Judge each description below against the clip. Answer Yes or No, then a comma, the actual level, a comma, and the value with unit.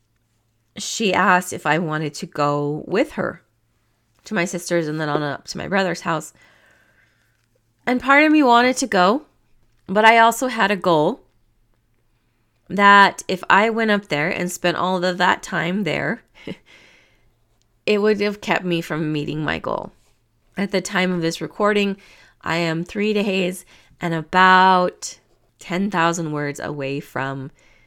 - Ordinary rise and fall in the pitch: No, wide, 7.7 semitones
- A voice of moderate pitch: Yes, medium, 170 Hz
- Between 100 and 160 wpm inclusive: Yes, average, 155 wpm